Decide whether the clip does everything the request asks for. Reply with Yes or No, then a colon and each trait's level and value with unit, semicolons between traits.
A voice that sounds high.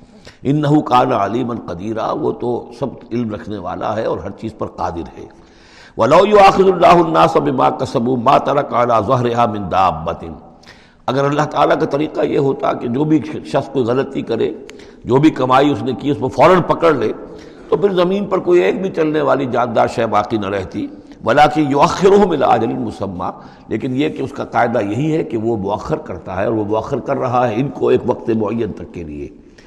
No: low, 125 Hz